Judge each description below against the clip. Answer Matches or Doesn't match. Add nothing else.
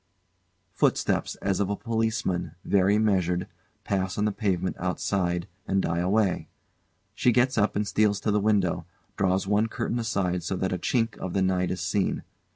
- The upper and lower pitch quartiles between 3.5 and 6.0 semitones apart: Doesn't match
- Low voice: Matches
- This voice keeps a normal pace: Matches